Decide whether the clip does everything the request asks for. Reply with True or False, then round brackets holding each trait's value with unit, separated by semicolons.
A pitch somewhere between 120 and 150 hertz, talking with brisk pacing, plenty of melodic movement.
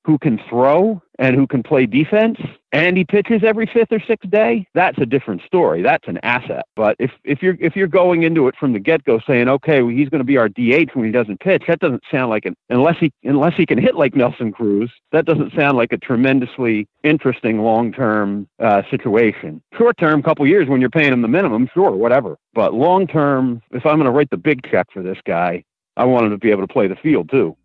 True (140 Hz; 240 wpm; 6.1 semitones)